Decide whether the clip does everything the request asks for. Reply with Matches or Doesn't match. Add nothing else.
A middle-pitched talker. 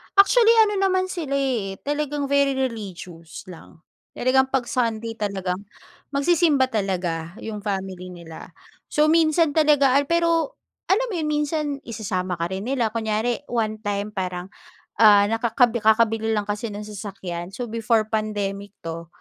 Doesn't match